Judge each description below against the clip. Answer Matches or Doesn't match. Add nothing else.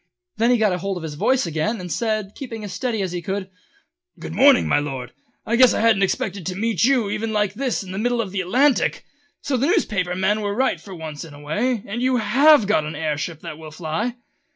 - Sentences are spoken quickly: Matches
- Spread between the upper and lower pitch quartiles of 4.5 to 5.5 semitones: Matches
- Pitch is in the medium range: Doesn't match